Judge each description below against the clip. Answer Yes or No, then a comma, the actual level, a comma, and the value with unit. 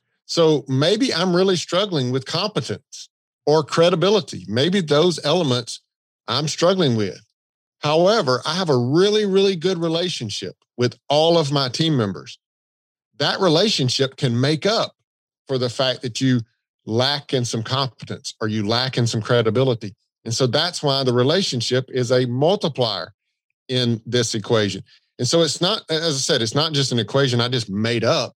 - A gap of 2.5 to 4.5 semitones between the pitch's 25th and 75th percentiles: No, average, 5.1 semitones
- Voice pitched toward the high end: No, low, 135 Hz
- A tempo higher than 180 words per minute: No, average, 165 wpm